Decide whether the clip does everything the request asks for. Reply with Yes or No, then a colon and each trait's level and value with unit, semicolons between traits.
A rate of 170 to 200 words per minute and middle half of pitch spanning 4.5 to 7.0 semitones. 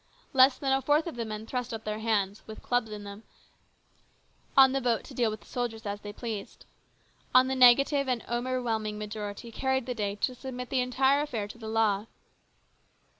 No: average, 195 wpm; average, 3.3 semitones